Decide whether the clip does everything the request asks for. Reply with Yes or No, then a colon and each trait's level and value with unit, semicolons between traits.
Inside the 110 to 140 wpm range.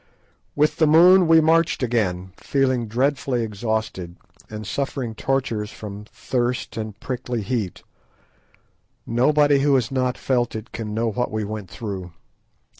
Yes: slow, 135 wpm